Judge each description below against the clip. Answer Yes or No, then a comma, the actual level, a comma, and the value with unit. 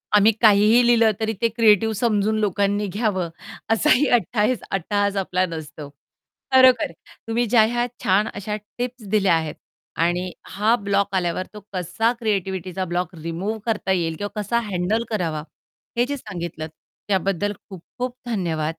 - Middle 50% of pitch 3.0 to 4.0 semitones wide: Yes, average, 3.7 semitones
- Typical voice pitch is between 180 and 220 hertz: Yes, high, 205 Hz